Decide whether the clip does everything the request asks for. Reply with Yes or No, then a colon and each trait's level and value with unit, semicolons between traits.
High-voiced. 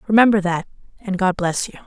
Yes: high, 195 Hz